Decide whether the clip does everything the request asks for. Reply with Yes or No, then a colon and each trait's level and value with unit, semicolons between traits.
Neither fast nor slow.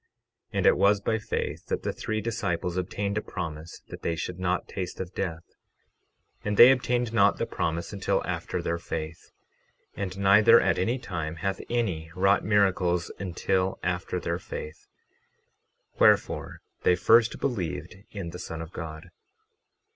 Yes: average, 160 wpm